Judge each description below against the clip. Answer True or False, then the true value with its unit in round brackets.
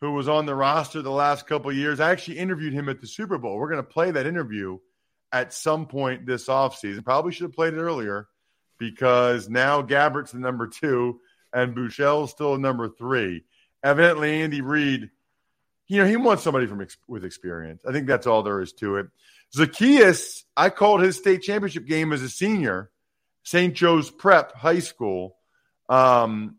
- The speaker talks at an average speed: True (185 wpm)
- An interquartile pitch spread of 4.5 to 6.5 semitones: True (5.0 semitones)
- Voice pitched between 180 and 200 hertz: False (140 Hz)